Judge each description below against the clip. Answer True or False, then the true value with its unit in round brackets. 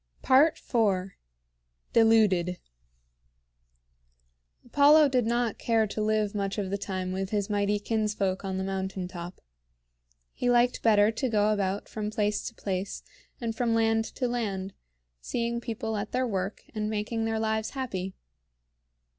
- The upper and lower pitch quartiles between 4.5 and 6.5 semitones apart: False (3.0 semitones)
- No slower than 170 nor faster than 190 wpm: False (140 wpm)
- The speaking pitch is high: True (215 Hz)